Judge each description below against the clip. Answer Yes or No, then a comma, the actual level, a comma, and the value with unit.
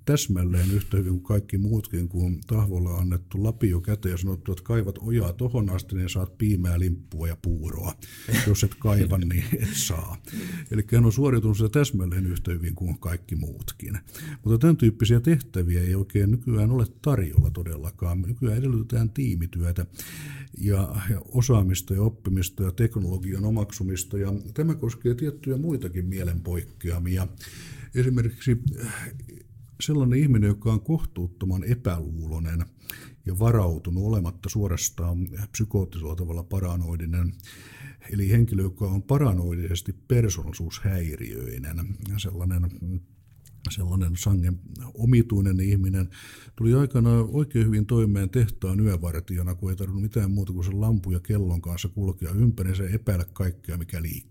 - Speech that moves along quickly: No, average, 130 wpm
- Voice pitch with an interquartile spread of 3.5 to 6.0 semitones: Yes, average, 4.4 semitones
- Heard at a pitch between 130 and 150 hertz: No, low, 100 Hz